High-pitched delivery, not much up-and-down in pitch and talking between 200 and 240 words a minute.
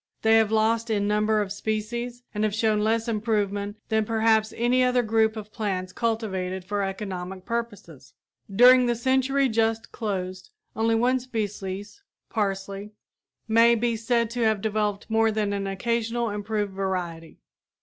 No: high, 220 Hz; narrow, 2.3 semitones; average, 150 wpm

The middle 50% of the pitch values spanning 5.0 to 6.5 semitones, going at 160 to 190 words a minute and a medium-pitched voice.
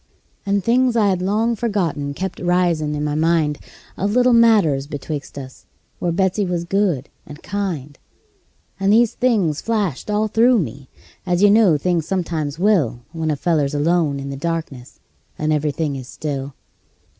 Yes: wide, 5.6 semitones; average, 165 wpm; medium, 170 Hz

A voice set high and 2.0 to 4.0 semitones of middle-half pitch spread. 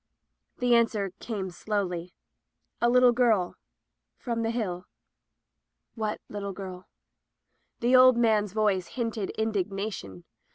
Yes: high, 215 Hz; average, 3.6 semitones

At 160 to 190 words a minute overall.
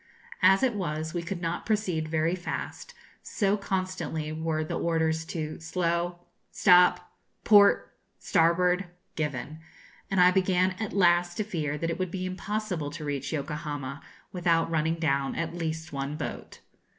No: average, 150 wpm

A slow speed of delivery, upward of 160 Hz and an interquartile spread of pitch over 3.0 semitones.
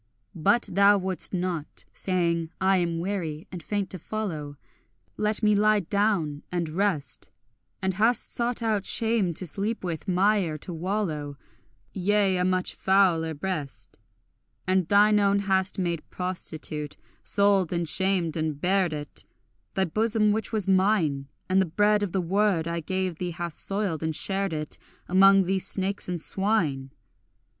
No: average, 150 wpm; medium, 185 Hz; average, 3.4 semitones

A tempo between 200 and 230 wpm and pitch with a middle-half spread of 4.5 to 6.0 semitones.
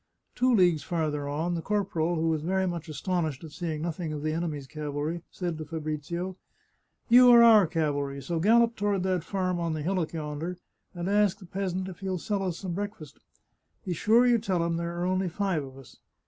No: fast, 205 wpm; average, 3.4 semitones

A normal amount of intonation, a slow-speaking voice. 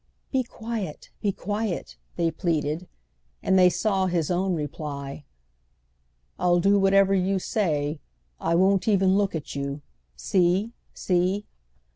Yes: average, 4.1 semitones; slow, 120 wpm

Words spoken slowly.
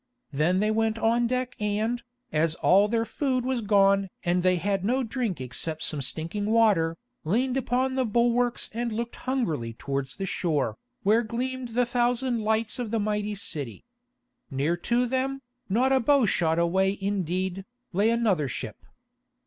No: average, 155 wpm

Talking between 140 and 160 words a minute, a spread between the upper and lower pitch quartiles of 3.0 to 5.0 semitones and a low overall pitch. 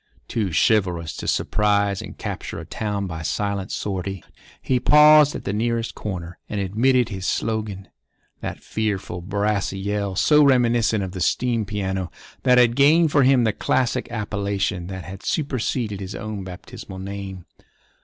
Yes: average, 150 wpm; average, 3.7 semitones; low, 105 Hz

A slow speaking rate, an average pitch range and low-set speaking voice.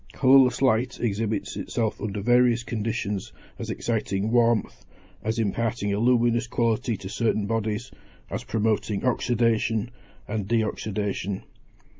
No: slow, 120 wpm; narrow, 2.2 semitones; low, 110 Hz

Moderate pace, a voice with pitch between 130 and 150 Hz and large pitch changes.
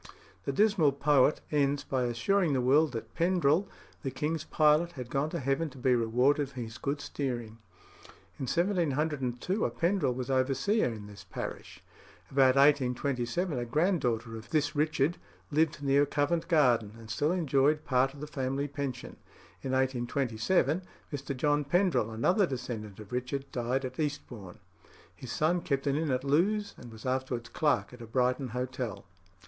No: average, 160 wpm; low, 135 Hz; average, 3.5 semitones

